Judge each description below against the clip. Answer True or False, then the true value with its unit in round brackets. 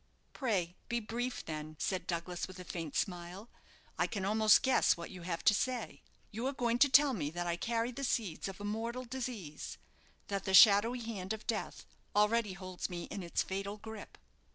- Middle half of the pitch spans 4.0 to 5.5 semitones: True (4.5 semitones)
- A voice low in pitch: False (205 Hz)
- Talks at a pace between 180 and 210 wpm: True (195 wpm)